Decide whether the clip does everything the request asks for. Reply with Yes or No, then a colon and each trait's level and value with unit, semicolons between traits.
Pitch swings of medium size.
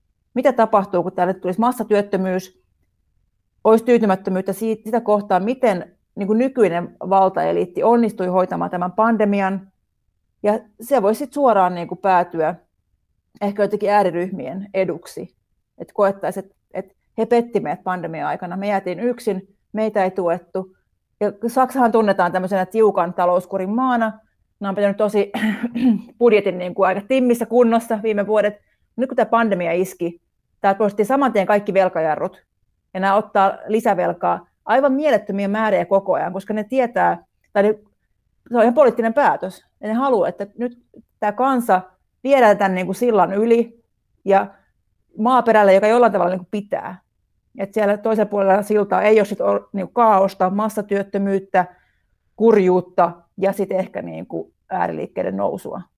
Yes: average, 3.2 semitones